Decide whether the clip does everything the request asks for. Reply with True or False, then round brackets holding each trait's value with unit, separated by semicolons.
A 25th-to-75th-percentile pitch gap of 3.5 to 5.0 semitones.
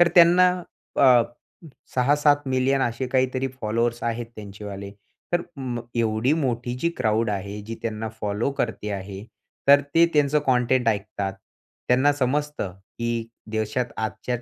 True (3.9 semitones)